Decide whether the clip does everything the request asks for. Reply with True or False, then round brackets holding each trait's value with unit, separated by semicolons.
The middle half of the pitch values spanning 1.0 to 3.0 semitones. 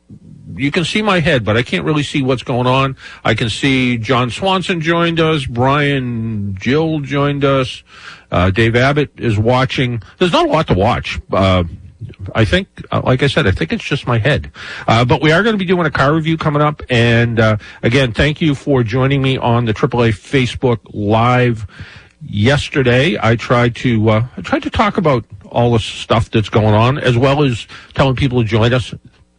False (4.2 semitones)